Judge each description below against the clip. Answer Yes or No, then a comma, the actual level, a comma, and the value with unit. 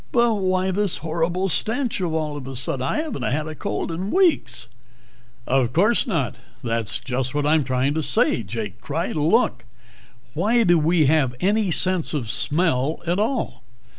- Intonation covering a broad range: Yes, wide, 6.4 semitones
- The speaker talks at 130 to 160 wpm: No, average, 170 wpm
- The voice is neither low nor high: Yes, medium, 160 Hz